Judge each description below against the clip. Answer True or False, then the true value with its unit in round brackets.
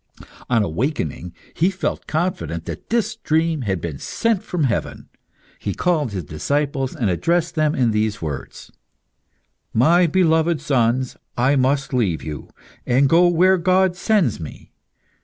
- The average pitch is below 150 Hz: True (140 Hz)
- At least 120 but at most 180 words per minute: True (140 wpm)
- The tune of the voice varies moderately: False (8.0 semitones)